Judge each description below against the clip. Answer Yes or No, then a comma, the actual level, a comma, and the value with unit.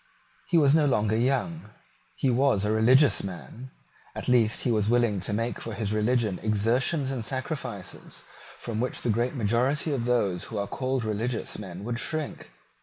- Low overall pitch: Yes, low, 120 Hz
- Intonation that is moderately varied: Yes, average, 3.6 semitones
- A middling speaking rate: Yes, average, 175 wpm